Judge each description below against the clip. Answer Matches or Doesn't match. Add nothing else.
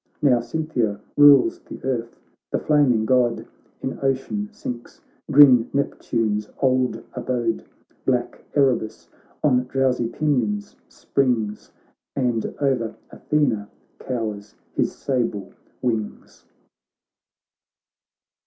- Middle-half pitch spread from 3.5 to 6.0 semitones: Doesn't match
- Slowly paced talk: Matches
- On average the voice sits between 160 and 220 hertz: Doesn't match